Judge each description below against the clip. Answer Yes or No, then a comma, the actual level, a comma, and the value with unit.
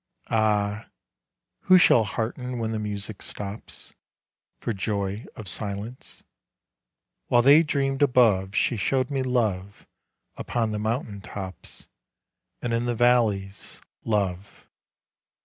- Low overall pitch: Yes, low, 110 Hz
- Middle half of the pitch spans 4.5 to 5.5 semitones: No, average, 3.4 semitones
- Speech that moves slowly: Yes, slow, 115 wpm